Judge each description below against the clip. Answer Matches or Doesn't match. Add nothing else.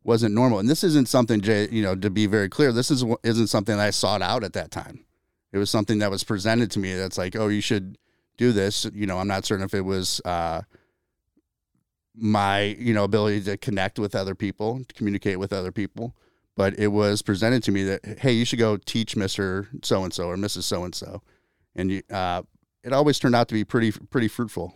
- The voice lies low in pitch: Matches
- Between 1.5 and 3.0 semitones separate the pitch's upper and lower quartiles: Matches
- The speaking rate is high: Matches